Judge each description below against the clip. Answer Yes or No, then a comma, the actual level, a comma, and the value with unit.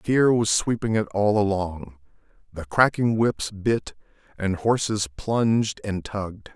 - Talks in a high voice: No, low, 100 Hz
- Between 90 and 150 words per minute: Yes, slow, 135 wpm